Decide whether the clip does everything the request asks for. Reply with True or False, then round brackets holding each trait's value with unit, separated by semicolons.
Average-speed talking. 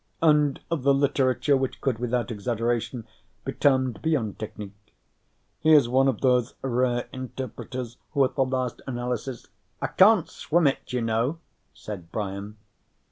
True (155 wpm)